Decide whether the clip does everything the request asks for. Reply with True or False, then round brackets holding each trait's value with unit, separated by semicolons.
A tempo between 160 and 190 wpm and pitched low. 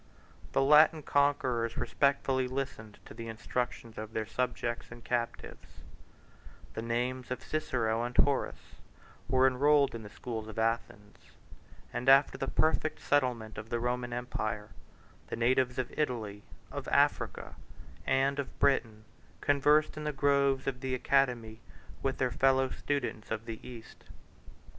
False (140 wpm; 125 Hz)